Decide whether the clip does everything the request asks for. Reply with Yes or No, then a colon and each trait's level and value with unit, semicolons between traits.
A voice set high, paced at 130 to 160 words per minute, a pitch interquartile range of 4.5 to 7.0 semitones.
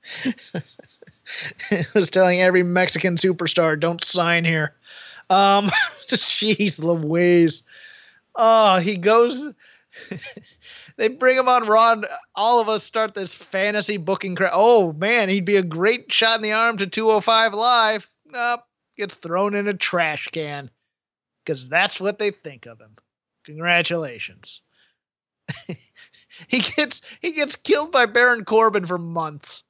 Yes: high, 205 Hz; slow, 135 wpm; average, 4.9 semitones